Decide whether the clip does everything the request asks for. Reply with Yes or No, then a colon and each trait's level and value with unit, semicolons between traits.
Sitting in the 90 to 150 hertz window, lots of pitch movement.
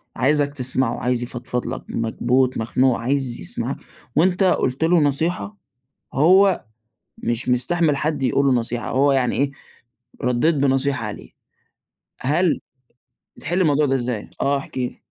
No: low, 135 Hz; average, 3.4 semitones